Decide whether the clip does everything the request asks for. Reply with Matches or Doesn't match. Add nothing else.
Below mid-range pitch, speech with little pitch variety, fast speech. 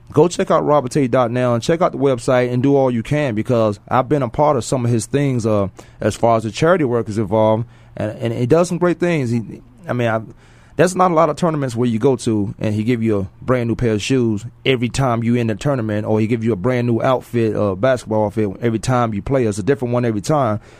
Doesn't match